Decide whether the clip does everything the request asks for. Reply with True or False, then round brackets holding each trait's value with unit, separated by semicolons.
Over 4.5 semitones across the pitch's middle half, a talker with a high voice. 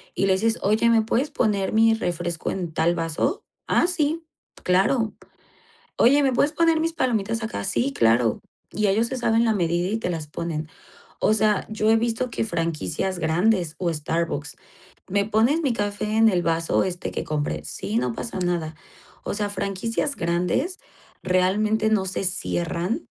True (4.9 semitones; 200 Hz)